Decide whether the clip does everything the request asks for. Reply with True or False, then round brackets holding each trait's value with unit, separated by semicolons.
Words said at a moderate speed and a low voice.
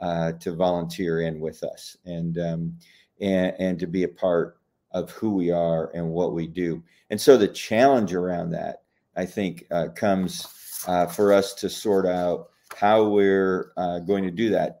True (180 wpm; 90 Hz)